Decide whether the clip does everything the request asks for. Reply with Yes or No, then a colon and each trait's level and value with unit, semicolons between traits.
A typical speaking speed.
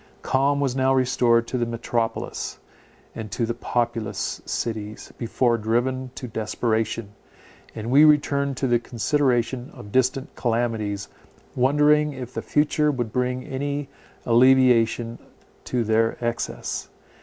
No: slow, 125 wpm